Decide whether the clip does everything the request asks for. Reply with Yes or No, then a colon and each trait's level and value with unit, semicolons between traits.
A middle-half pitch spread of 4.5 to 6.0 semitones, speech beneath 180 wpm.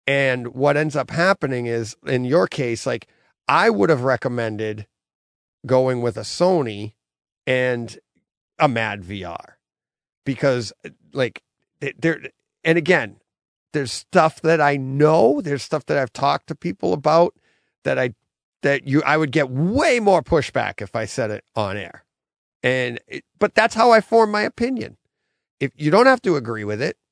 Yes: average, 5.1 semitones; average, 160 wpm